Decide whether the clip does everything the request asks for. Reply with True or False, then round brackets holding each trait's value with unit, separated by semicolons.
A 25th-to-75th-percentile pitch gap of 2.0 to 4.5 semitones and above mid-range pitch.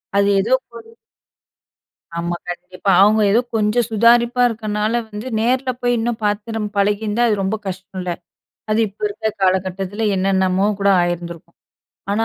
True (2.9 semitones; 210 Hz)